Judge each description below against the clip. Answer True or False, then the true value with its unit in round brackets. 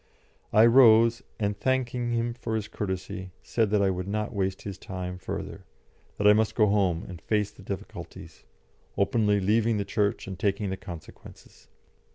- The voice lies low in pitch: True (105 Hz)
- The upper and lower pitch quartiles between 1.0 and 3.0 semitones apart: True (2.7 semitones)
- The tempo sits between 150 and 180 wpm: True (170 wpm)